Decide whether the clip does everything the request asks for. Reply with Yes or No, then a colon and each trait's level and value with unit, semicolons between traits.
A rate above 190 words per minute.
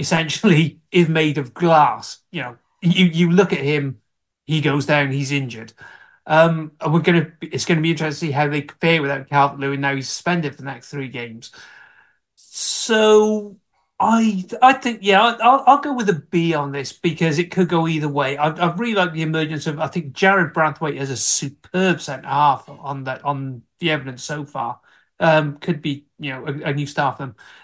Yes: fast, 205 wpm